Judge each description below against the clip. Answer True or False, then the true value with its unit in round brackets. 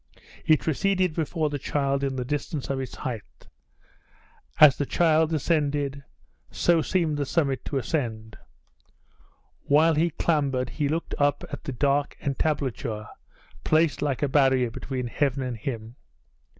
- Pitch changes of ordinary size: True (3.0 semitones)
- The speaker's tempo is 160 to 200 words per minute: False (140 wpm)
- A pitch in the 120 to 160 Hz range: True (140 Hz)